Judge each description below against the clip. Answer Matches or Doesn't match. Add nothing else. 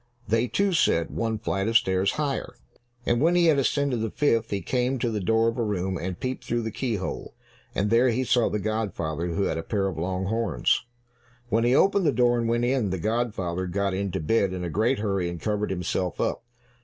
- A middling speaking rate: Doesn't match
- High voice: Doesn't match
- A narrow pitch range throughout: Doesn't match